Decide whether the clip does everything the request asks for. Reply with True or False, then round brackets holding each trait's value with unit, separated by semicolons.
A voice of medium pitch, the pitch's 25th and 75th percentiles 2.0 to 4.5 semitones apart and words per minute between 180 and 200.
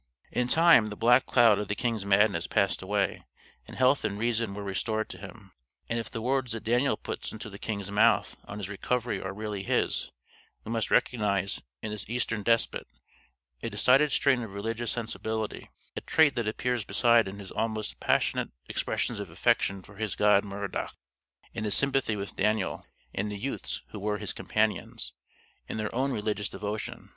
False (110 Hz; 2.6 semitones; 185 wpm)